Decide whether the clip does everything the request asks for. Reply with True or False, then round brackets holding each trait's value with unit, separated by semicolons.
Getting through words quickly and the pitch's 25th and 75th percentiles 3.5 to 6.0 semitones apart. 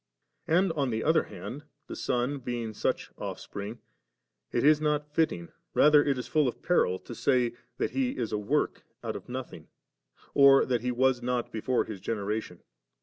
False (175 wpm; 4.6 semitones)